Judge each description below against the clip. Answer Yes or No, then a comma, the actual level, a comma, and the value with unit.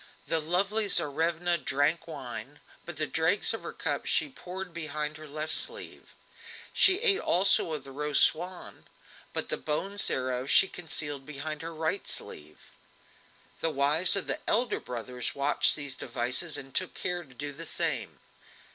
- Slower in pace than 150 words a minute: No, average, 160 wpm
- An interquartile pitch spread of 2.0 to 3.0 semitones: No, average, 3.9 semitones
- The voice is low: No, medium, 155 Hz